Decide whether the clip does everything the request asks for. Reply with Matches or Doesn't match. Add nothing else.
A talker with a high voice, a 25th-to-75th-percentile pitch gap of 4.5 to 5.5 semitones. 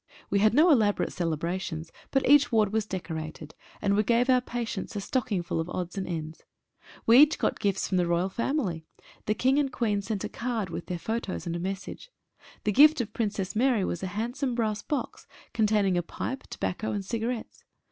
Matches